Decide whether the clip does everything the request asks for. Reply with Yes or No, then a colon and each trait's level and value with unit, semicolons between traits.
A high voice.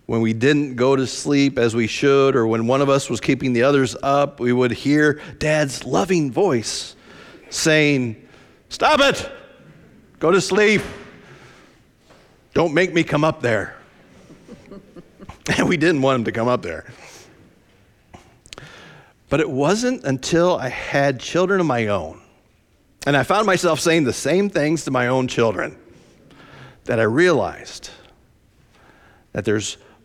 No: medium, 140 Hz